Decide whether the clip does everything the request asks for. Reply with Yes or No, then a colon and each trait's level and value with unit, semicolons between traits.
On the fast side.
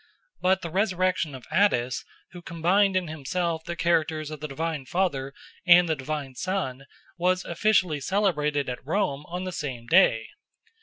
No: average, 155 wpm